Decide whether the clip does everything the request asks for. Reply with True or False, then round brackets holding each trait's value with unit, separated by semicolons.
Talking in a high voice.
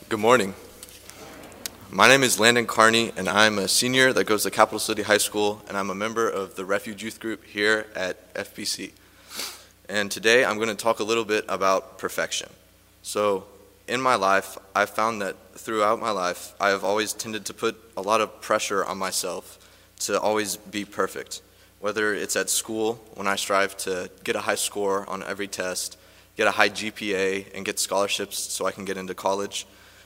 False (105 Hz)